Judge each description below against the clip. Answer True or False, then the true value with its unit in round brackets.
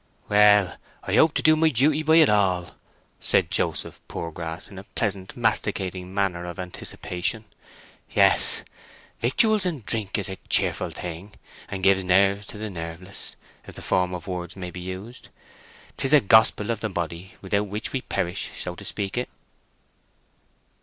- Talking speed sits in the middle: True (160 wpm)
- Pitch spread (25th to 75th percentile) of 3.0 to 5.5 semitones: True (3.5 semitones)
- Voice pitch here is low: True (100 Hz)